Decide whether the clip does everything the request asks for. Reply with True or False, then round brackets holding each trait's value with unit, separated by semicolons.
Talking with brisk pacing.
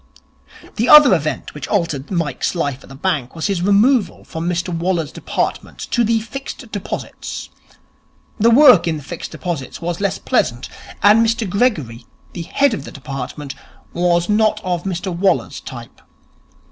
False (160 wpm)